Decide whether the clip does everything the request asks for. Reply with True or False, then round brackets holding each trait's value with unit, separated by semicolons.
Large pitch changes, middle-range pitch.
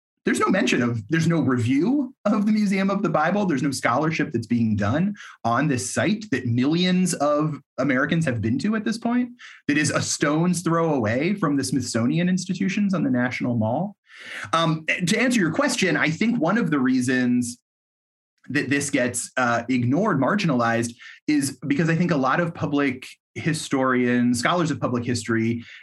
True (6.8 semitones; 150 Hz)